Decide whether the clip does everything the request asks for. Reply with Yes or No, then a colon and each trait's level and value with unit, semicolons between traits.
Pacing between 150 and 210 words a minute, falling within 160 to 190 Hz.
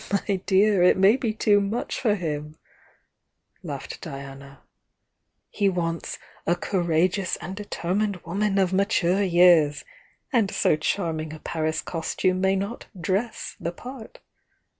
No: average, 140 wpm; medium, 185 Hz